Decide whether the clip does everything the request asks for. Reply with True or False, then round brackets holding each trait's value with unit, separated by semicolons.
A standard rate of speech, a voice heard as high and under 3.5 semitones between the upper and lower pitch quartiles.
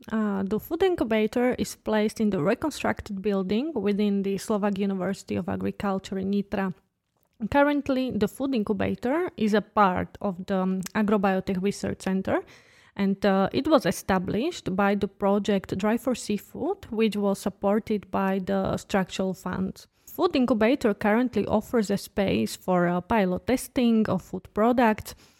True (145 wpm; 205 Hz; 2.8 semitones)